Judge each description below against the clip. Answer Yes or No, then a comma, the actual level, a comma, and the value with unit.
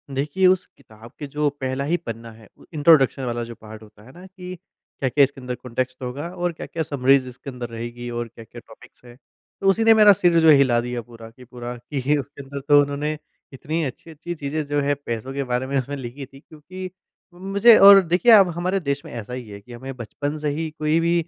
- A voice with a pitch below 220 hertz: Yes, medium, 140 Hz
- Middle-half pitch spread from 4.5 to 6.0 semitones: Yes, average, 4.9 semitones